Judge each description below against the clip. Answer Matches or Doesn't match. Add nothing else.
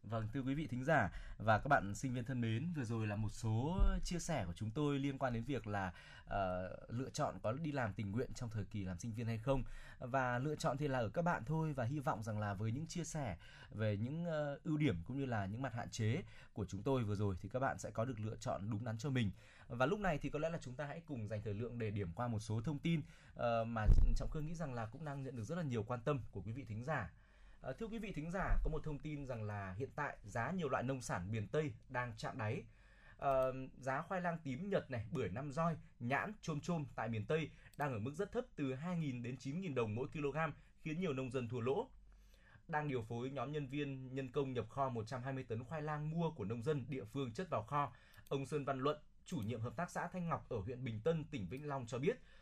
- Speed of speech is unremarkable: Doesn't match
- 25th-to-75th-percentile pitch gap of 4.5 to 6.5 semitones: Matches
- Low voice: Matches